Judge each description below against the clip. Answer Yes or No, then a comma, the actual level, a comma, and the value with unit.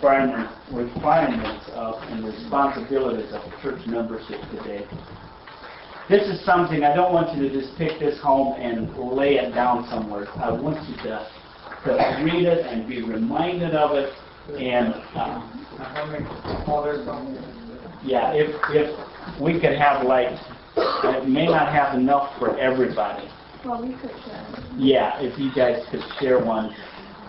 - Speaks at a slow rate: Yes, slow, 130 wpm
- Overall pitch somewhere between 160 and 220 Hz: No, low, 135 Hz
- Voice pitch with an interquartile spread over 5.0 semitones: No, average, 3.8 semitones